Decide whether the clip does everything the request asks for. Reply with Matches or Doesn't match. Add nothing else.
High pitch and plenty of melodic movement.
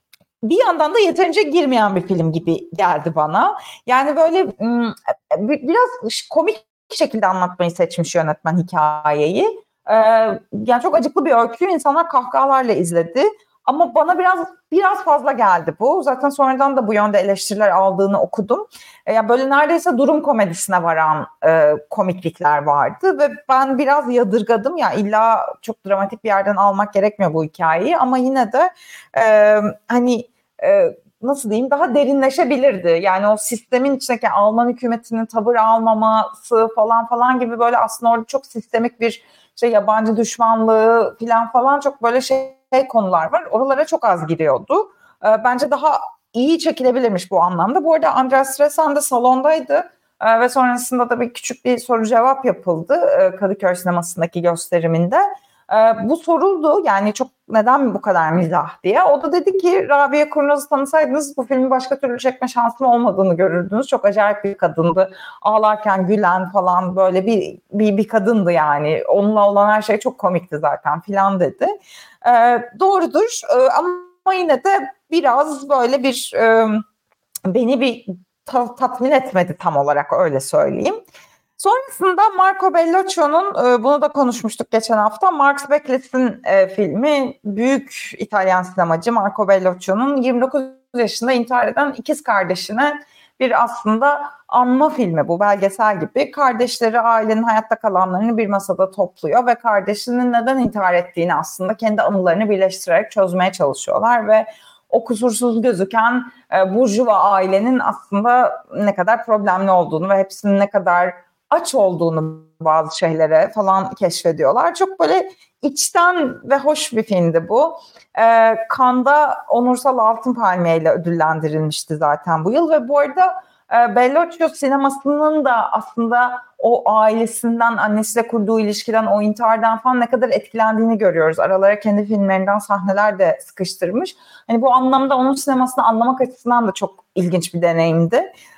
Matches